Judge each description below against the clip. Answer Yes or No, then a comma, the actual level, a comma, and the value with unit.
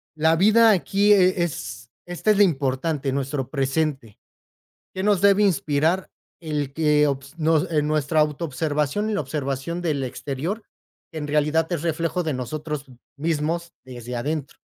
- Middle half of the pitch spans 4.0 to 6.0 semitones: No, average, 3.6 semitones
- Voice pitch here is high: No, medium, 155 Hz